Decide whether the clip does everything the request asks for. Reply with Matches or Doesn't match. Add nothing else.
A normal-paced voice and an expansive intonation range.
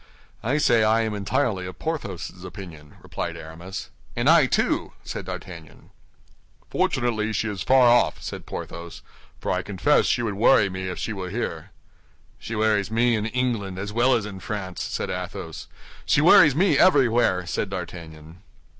Doesn't match